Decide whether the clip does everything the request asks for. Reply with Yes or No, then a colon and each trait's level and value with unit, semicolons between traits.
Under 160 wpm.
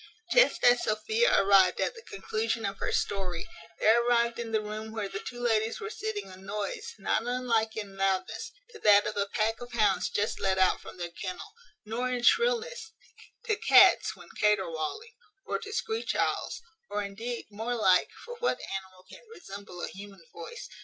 No: average, 180 wpm